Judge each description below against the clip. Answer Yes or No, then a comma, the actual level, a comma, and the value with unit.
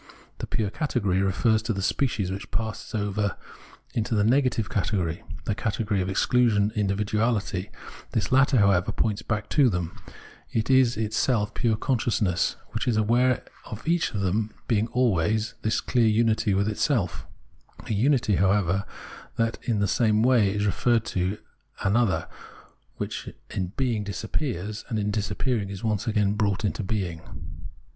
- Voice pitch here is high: No, low, 105 Hz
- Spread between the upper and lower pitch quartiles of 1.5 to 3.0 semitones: Yes, average, 2.7 semitones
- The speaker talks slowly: No, average, 160 wpm